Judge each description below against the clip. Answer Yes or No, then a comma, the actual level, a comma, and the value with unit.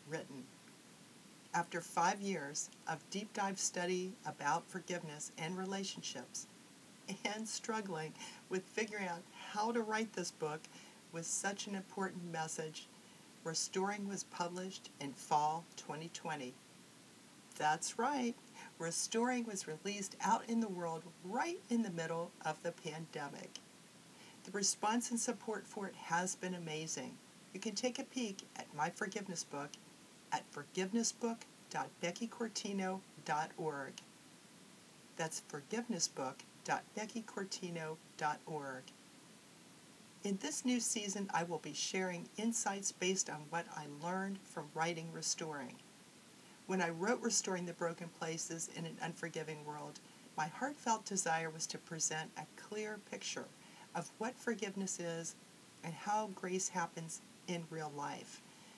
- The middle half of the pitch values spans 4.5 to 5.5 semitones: Yes, average, 4.8 semitones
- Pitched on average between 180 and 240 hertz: Yes, medium, 185 Hz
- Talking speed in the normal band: No, slow, 120 wpm